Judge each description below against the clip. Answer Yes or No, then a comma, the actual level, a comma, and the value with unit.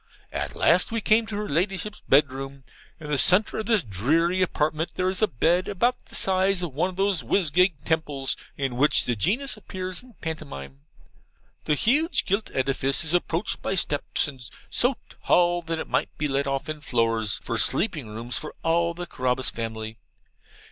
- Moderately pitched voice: Yes, medium, 160 Hz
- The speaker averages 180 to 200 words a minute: Yes, average, 185 wpm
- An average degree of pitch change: No, wide, 5.7 semitones